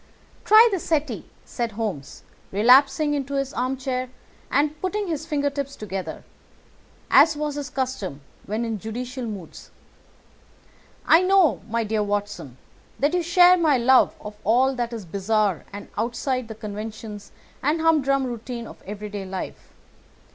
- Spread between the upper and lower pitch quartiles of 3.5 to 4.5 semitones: No, wide, 5.4 semitones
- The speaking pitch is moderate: No, very high, 250 Hz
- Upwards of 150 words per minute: No, average, 140 wpm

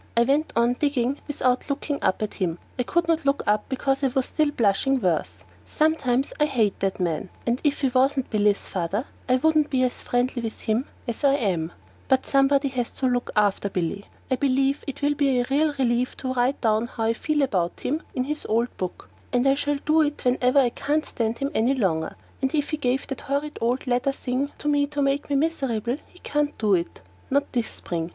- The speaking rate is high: Yes, fast, 215 wpm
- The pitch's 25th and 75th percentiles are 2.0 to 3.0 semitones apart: No, average, 3.8 semitones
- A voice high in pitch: Yes, very high, 255 Hz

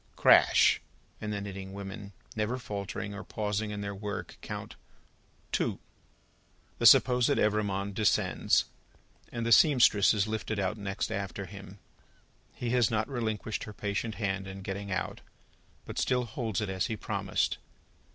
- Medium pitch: No, low, 105 Hz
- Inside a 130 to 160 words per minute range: Yes, average, 145 wpm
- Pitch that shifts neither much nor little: No, narrow, 1.9 semitones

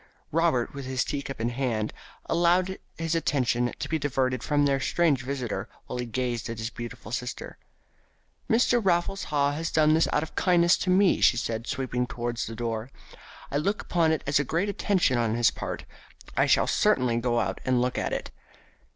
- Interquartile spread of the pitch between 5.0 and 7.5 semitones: Yes, average, 5.3 semitones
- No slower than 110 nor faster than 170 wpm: No, average, 195 wpm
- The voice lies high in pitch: No, low, 135 Hz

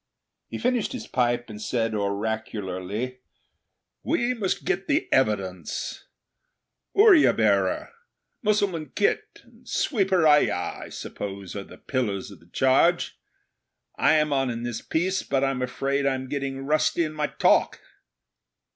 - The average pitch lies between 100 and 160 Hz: Yes, low, 135 Hz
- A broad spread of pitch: Yes, wide, 7.7 semitones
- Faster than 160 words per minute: No, average, 140 wpm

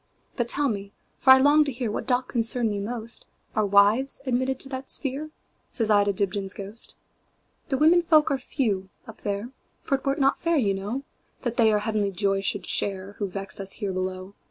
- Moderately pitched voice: No, high, 225 Hz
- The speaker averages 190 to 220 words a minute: No, average, 180 wpm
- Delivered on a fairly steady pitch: No, average, 4.9 semitones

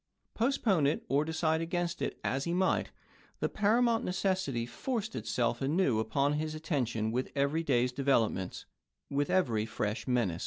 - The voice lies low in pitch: No, medium, 145 Hz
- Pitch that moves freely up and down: Yes, wide, 6.7 semitones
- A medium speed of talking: Yes, average, 155 wpm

